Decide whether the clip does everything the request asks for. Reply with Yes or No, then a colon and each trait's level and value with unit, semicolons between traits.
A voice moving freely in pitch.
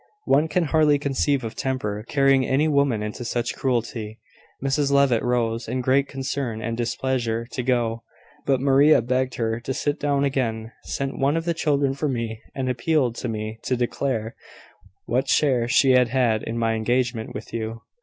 No: average, 3.2 semitones